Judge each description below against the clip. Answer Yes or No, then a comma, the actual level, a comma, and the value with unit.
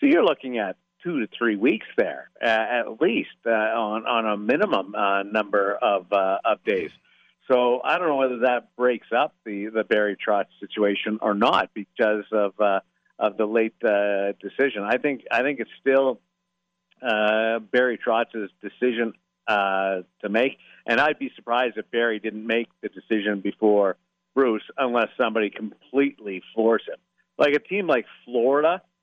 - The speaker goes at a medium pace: Yes, average, 165 wpm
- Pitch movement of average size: Yes, average, 3.0 semitones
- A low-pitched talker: Yes, low, 110 Hz